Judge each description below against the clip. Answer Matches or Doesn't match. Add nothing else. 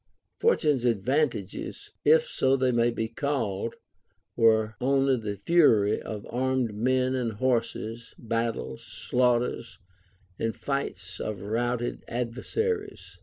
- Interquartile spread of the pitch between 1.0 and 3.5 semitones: Matches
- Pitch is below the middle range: Matches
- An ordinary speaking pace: Doesn't match